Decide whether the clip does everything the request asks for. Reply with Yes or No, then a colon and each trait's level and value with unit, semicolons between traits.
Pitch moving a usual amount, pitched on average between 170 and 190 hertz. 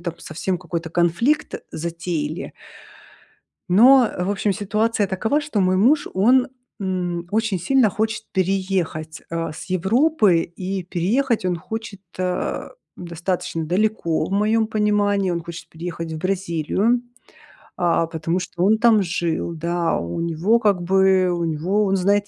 Yes: average, 3.8 semitones; medium, 185 Hz